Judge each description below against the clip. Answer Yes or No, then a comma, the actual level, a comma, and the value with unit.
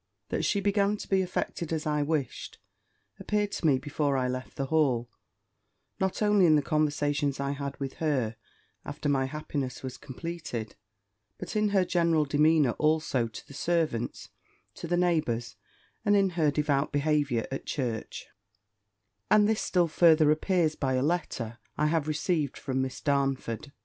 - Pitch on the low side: No, medium, 150 Hz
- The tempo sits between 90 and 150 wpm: No, average, 160 wpm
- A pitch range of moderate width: Yes, average, 3.9 semitones